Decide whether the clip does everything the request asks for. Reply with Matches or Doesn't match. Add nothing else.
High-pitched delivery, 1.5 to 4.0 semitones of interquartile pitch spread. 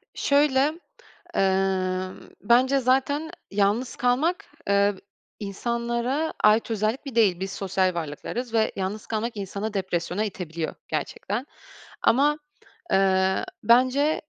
Doesn't match